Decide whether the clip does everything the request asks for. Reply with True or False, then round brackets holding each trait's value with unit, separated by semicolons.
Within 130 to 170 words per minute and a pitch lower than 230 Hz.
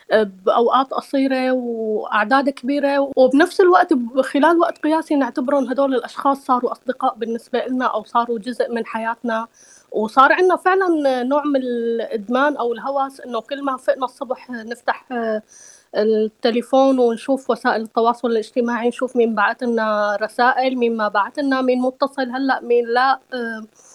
False (135 wpm; 250 Hz)